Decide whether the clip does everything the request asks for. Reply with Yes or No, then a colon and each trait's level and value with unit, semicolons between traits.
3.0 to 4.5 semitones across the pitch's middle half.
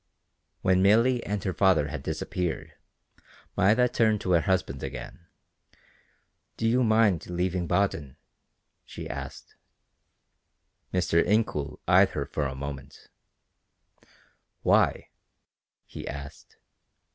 No: wide, 5.4 semitones